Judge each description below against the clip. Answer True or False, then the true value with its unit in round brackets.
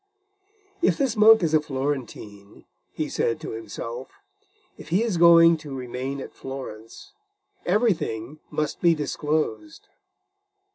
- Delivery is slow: True (125 wpm)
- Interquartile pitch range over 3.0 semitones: True (5.1 semitones)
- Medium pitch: True (150 Hz)